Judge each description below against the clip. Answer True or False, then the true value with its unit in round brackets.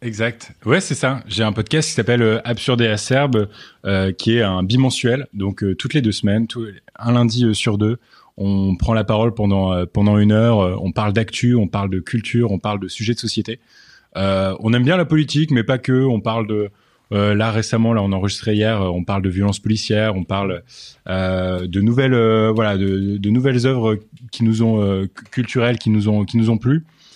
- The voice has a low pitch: True (110 Hz)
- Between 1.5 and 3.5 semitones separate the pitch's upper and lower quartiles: True (3.1 semitones)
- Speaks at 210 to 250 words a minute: True (215 wpm)